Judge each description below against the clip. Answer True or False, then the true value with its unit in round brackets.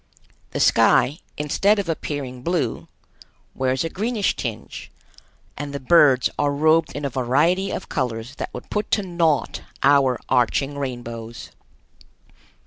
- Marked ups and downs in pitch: False (4.5 semitones)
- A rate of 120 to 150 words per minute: True (135 wpm)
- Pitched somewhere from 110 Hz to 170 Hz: True (140 Hz)